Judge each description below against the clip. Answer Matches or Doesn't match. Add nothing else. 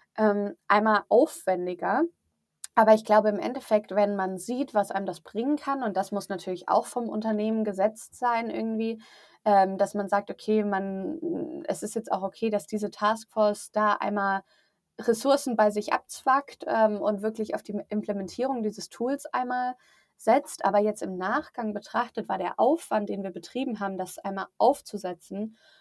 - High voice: Matches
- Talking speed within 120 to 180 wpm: Matches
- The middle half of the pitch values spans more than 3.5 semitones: Doesn't match